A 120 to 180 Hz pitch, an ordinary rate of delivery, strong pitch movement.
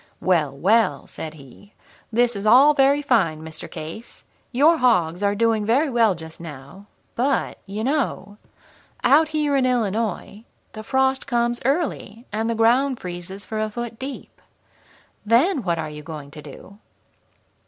No: high, 220 Hz; average, 155 wpm; wide, 6.6 semitones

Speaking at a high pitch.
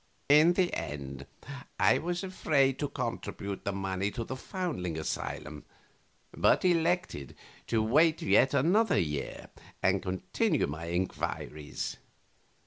No: low, 115 Hz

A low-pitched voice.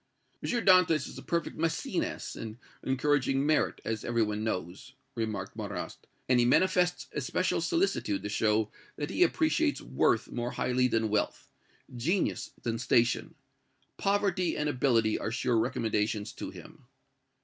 Yes: low, 120 Hz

